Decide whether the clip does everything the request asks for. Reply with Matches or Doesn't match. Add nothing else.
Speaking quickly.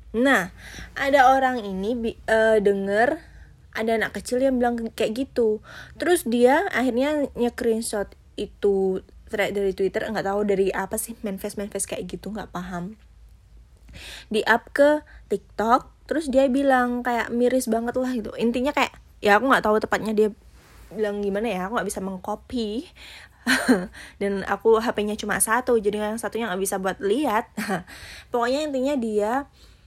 Matches